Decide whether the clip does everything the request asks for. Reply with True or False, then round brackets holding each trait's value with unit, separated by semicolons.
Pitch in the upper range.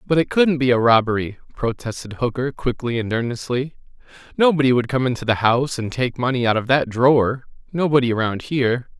False (125 Hz)